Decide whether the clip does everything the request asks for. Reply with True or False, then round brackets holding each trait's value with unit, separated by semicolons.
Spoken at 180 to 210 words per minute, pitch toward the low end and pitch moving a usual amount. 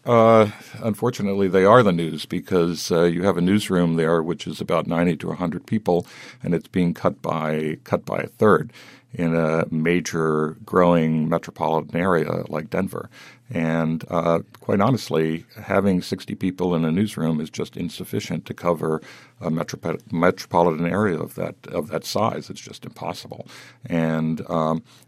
False (165 wpm; 85 Hz; 3.4 semitones)